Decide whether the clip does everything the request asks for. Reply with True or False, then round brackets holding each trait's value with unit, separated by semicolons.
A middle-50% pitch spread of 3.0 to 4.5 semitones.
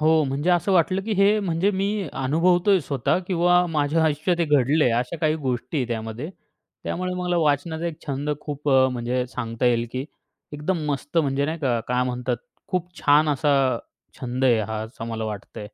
False (5.3 semitones)